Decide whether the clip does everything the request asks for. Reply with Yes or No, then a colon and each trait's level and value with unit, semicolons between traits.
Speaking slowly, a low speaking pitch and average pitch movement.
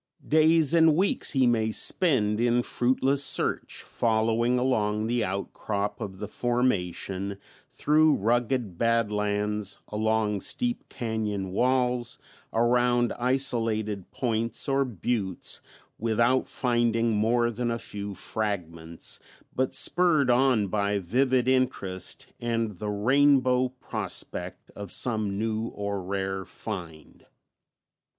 Yes: slow, 110 wpm; low, 115 Hz; average, 3.5 semitones